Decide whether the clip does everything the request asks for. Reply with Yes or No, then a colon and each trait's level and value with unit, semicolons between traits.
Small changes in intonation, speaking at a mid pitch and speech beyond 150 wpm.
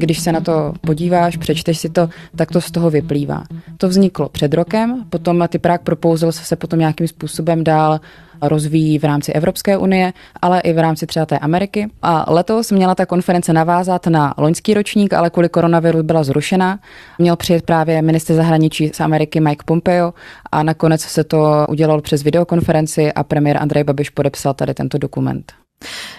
Yes: narrow, 2.0 semitones; medium, 165 Hz; fast, 170 wpm